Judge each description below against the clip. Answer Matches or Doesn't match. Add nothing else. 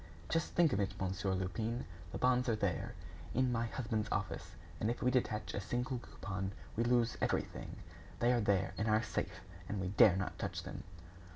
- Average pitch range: Matches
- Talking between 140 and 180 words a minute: Doesn't match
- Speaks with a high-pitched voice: Doesn't match